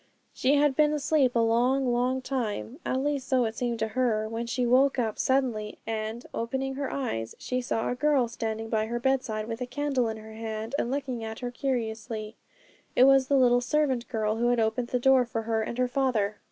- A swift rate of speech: Yes, fast, 215 wpm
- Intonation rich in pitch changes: No, average, 3.0 semitones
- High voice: Yes, high, 245 Hz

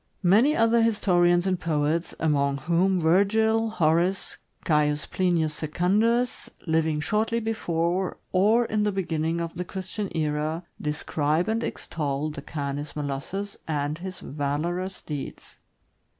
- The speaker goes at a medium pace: No, slow, 125 wpm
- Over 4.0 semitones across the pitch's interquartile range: Yes, average, 4.5 semitones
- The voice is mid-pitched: Yes, medium, 170 Hz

